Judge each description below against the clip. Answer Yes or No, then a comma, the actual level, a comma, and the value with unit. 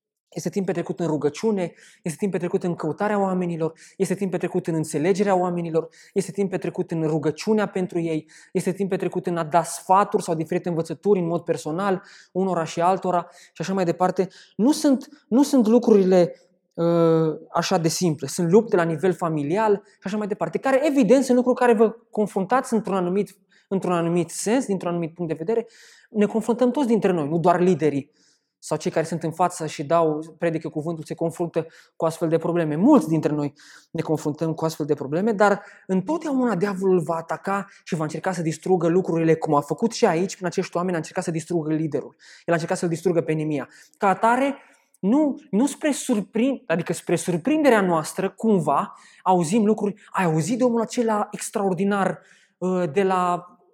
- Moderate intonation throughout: Yes, average, 3.7 semitones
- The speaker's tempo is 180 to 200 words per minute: Yes, average, 185 wpm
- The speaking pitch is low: No, medium, 180 Hz